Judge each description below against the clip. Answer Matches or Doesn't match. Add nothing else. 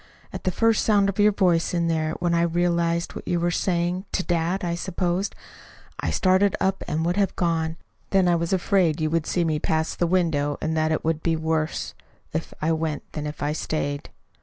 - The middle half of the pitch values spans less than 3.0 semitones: Matches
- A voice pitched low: Doesn't match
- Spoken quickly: Matches